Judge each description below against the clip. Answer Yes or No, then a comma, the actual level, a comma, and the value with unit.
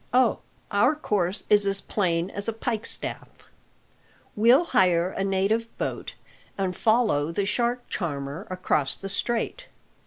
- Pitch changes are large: No, average, 4.0 semitones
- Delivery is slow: Yes, slow, 130 wpm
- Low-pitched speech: No, high, 200 Hz